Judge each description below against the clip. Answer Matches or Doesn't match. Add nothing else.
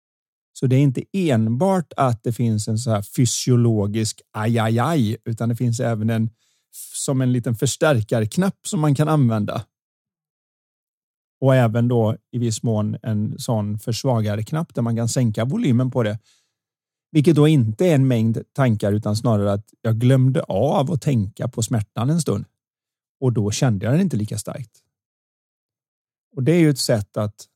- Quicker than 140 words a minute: Matches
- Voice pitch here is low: Matches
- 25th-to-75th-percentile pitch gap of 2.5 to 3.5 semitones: Doesn't match